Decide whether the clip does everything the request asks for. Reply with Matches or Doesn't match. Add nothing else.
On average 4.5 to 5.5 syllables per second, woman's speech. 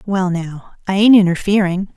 Matches